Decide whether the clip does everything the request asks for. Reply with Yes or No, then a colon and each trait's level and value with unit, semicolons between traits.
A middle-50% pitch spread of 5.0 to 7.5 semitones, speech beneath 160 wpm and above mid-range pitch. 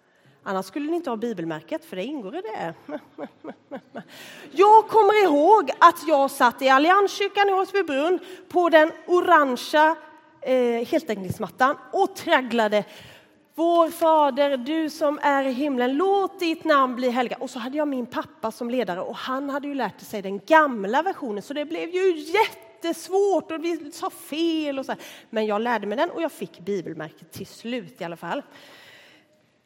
No: wide, 5.5 semitones; average, 165 wpm; very high, 295 Hz